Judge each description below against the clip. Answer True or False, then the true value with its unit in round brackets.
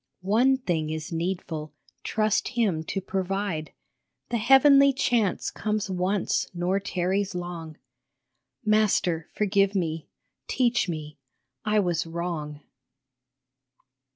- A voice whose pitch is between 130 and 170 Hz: False (190 Hz)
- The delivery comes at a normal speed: False (105 wpm)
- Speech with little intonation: False (4.5 semitones)